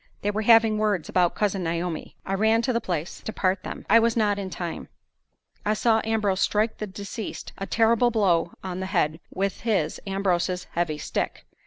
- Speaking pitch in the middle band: No, high, 200 Hz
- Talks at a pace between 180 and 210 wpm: Yes, average, 190 wpm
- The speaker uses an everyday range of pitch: Yes, average, 3.4 semitones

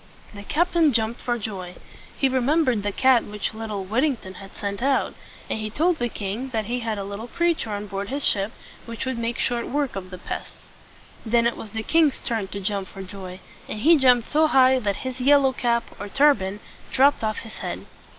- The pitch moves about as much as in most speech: Yes, average, 4.5 semitones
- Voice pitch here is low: No, high, 230 Hz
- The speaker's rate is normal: No, fast, 210 wpm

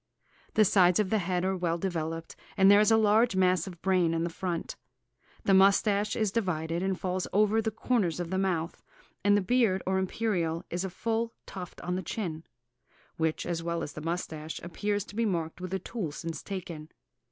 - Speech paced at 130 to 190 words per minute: No, average, 200 wpm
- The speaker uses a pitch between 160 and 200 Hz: Yes, medium, 185 Hz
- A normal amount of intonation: Yes, average, 3.4 semitones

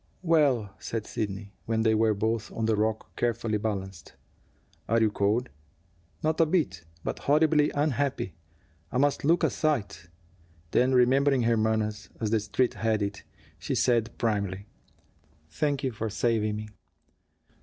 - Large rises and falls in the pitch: No, average, 4.0 semitones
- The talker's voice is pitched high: No, low, 115 Hz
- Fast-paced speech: No, average, 145 wpm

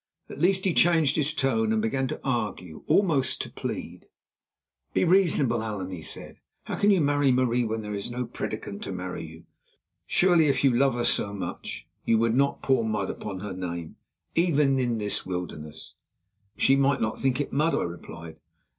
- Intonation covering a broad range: Yes, wide, 5.7 semitones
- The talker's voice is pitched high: No, low, 120 Hz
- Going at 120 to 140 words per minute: No, average, 185 wpm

